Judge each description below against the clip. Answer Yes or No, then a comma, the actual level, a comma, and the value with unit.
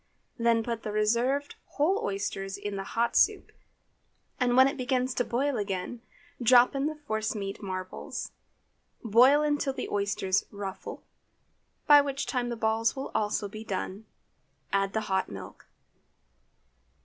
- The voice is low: No, high, 225 Hz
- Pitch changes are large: No, average, 4.5 semitones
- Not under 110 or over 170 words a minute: Yes, average, 145 wpm